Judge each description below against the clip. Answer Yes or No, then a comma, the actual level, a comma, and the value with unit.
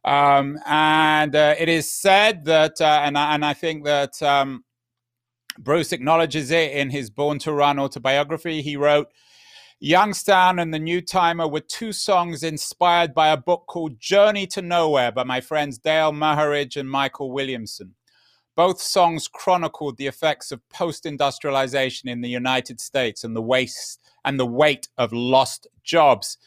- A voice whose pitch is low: No, medium, 150 Hz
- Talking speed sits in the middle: Yes, average, 160 wpm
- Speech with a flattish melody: No, average, 3.2 semitones